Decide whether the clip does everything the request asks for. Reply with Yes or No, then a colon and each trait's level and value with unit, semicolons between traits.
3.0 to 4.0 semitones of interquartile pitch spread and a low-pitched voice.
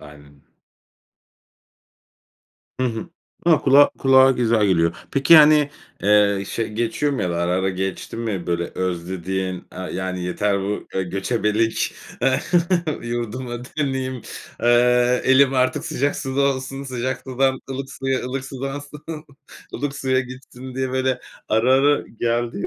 No: average, 5.0 semitones; low, 125 Hz